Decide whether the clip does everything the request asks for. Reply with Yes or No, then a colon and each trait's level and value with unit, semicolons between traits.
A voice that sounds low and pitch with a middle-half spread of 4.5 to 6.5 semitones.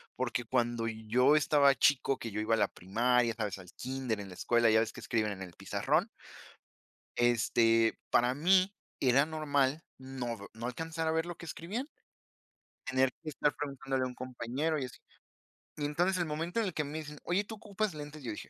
Yes: low, 130 Hz; average, 4.9 semitones